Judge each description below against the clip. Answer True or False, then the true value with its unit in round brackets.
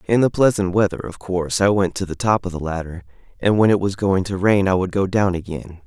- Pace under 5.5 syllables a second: False (5.9 syllables/s)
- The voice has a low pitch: True (95 Hz)